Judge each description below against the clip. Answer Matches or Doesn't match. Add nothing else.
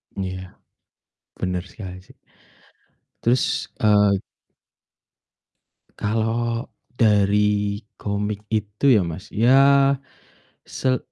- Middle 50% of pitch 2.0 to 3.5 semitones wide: Matches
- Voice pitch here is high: Doesn't match